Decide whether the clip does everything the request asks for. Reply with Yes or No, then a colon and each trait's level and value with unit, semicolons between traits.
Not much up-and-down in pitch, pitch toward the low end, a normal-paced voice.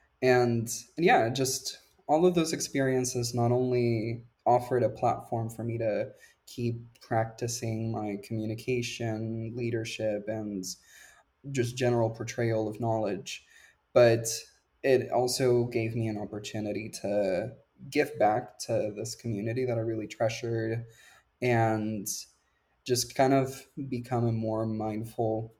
No: narrow, 1.7 semitones; low, 115 Hz; slow, 120 wpm